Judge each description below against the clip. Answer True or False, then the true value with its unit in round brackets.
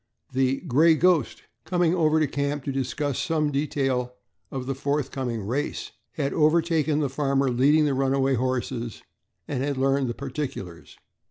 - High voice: False (140 Hz)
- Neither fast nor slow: True (155 wpm)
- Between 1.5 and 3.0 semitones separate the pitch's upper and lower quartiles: True (2.6 semitones)